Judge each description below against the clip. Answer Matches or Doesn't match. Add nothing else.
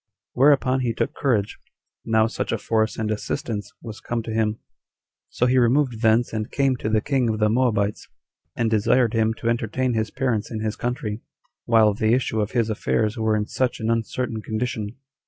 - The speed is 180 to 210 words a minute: Matches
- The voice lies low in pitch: Matches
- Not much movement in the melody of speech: Matches